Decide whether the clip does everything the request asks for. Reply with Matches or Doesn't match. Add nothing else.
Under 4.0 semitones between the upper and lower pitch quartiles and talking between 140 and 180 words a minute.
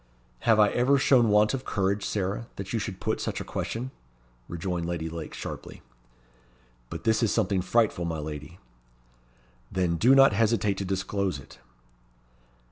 Doesn't match